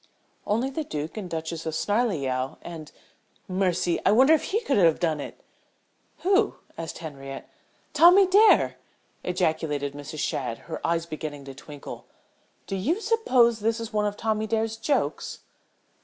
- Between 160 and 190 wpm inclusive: No, average, 150 wpm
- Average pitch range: No, wide, 7.0 semitones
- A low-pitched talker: No, medium, 185 Hz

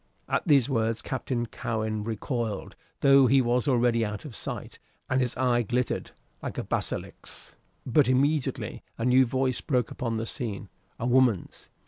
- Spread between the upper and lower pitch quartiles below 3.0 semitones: Yes, narrow, 2.4 semitones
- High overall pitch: No, low, 125 Hz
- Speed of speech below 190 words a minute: Yes, average, 155 wpm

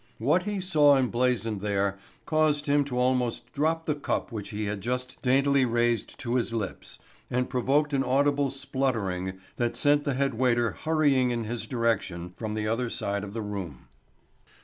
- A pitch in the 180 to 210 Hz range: No, low, 125 Hz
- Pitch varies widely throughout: No, average, 4.1 semitones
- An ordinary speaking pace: Yes, average, 170 wpm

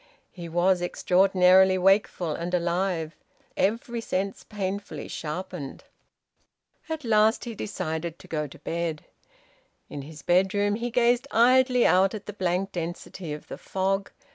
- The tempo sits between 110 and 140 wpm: Yes, slow, 135 wpm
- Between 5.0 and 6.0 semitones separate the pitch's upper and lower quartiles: No, average, 3.3 semitones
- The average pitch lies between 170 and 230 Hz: Yes, medium, 185 Hz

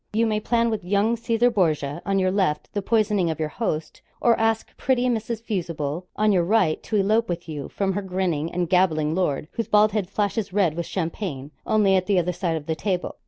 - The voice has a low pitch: No, high, 190 Hz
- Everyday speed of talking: No, fast, 215 wpm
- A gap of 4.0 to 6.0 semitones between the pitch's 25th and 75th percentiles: Yes, average, 4.5 semitones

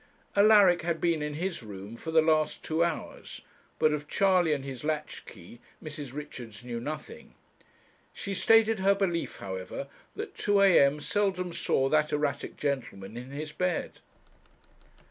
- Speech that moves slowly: No, average, 150 wpm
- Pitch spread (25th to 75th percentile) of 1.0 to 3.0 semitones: No, average, 5.1 semitones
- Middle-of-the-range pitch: Yes, medium, 155 Hz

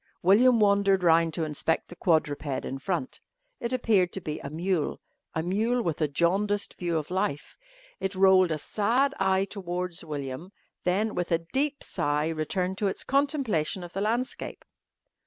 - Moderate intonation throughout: Yes, average, 4.1 semitones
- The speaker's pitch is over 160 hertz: Yes, medium, 185 Hz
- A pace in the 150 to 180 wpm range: Yes, average, 165 wpm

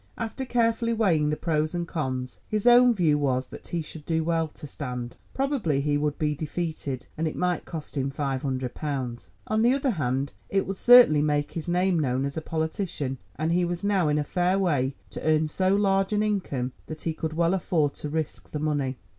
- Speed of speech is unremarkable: No, fast, 215 wpm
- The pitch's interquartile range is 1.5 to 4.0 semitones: No, average, 4.6 semitones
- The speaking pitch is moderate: Yes, medium, 160 Hz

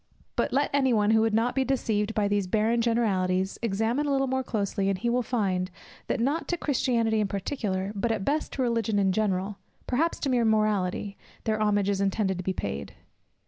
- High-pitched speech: Yes, high, 220 Hz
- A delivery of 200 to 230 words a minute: Yes, fast, 205 wpm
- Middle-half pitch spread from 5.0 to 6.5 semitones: No, average, 3.7 semitones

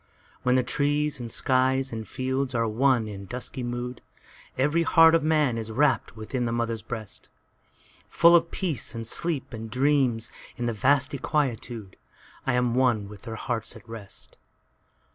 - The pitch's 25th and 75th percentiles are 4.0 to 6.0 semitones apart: No, average, 3.4 semitones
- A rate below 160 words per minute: Yes, average, 150 wpm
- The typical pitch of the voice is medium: No, low, 125 Hz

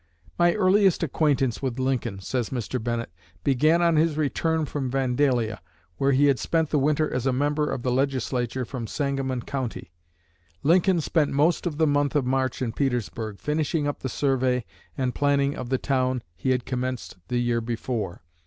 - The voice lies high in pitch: No, low, 135 Hz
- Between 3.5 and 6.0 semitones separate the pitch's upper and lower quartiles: No, average, 3.0 semitones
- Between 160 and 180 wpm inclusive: Yes, average, 175 wpm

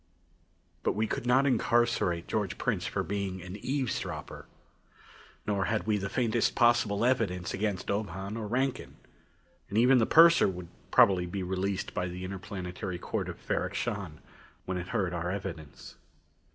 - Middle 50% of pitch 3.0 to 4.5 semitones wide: Yes, average, 4.1 semitones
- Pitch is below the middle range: Yes, low, 100 Hz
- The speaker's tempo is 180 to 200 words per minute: No, average, 155 wpm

